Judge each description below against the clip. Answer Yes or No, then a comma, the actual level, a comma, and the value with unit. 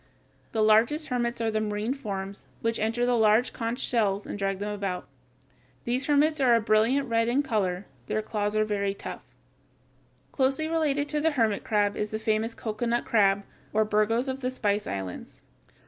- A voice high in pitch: Yes, high, 220 Hz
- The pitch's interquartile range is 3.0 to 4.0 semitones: Yes, average, 3.3 semitones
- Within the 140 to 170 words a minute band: No, average, 180 wpm